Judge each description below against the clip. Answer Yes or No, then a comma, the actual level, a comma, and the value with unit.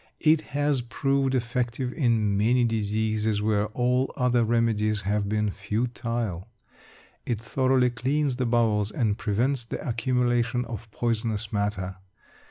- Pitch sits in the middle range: No, low, 115 Hz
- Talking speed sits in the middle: No, slow, 125 wpm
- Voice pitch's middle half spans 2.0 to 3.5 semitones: Yes, average, 2.8 semitones